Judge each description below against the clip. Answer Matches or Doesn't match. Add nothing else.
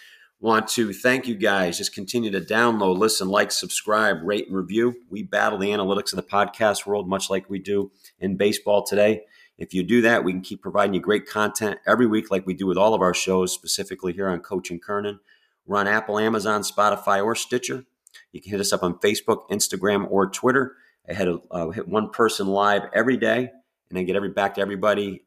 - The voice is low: Matches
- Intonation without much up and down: Matches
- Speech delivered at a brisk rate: Matches